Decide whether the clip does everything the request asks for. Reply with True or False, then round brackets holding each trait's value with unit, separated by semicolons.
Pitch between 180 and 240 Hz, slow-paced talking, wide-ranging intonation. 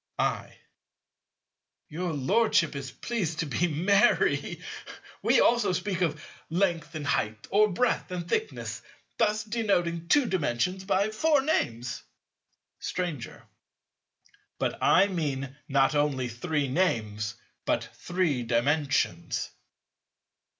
False (170 Hz; 110 wpm; 6.2 semitones)